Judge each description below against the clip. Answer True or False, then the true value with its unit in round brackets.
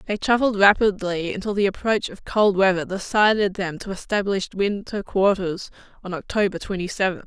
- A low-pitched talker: False (195 Hz)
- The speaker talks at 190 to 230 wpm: False (155 wpm)